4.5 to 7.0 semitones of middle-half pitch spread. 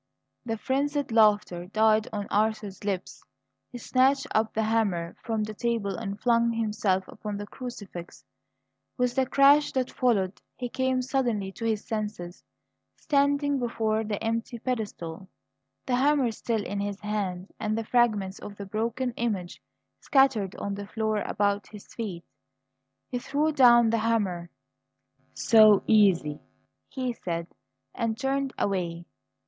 No: average, 3.4 semitones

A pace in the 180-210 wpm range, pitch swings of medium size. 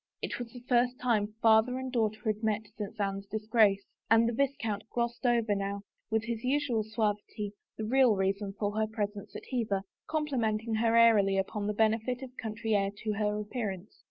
No: average, 185 wpm; narrow, 2.3 semitones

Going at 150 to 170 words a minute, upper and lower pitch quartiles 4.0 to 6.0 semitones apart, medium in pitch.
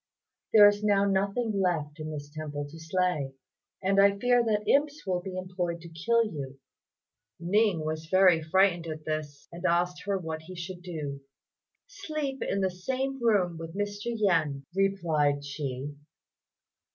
Yes: average, 155 wpm; average, 4.4 semitones; medium, 180 Hz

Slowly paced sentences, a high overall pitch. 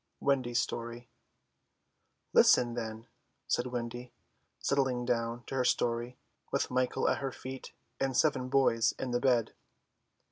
No: slow, 130 wpm; low, 125 Hz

